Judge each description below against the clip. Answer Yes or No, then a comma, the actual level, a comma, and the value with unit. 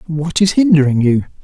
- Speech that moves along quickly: No, average, 165 wpm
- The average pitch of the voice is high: No, medium, 155 Hz